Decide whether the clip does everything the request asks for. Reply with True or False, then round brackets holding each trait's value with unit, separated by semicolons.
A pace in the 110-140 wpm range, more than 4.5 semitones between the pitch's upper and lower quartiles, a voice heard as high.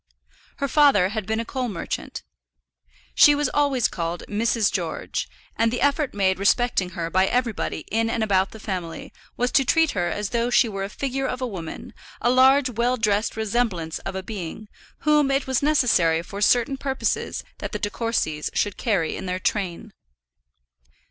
False (180 wpm; 5.1 semitones; 220 Hz)